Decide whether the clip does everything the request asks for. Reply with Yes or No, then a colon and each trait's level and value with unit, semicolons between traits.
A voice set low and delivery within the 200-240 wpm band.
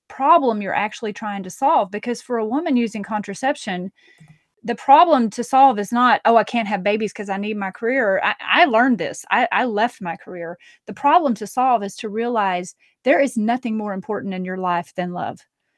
No: high, 215 Hz; fast, 205 wpm